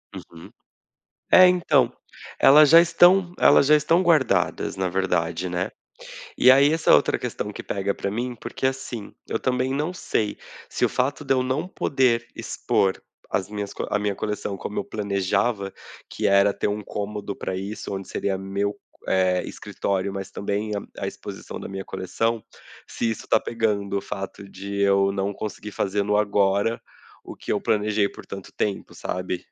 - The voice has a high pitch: No, low, 105 Hz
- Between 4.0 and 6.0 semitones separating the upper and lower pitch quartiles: Yes, average, 4.4 semitones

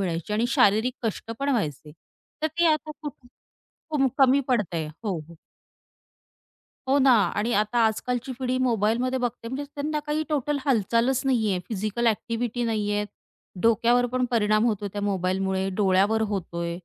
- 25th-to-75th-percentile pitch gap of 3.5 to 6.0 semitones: Yes, average, 3.9 semitones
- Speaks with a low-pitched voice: No, high, 230 Hz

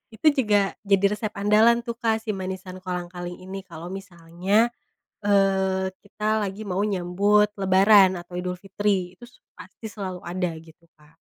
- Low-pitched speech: No, high, 190 Hz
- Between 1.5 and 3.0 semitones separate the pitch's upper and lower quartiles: Yes, narrow, 2.5 semitones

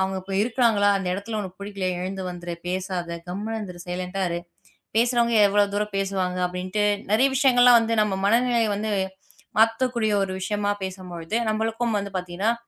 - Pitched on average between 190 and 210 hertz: Yes, high, 200 Hz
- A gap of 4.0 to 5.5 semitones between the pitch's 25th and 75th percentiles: No, average, 3.5 semitones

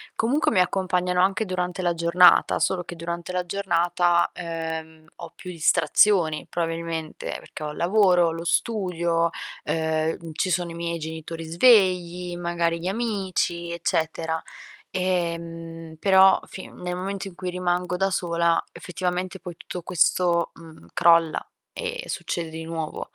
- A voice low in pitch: No, medium, 175 Hz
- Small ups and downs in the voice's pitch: Yes, narrow, 1.7 semitones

